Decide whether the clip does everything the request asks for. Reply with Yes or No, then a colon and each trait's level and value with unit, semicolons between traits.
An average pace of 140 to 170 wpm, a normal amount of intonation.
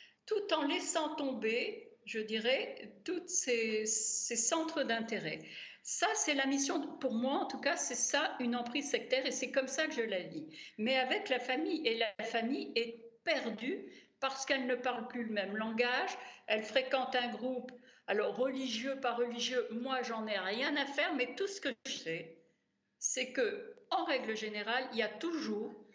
No: average, 185 wpm; average, 3.8 semitones